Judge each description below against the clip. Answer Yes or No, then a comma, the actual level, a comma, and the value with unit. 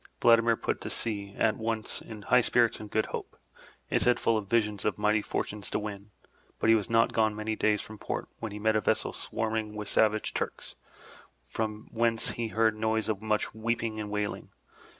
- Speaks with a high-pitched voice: No, low, 110 Hz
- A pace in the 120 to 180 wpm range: No, average, 200 wpm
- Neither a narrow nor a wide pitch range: No, narrow, 1.1 semitones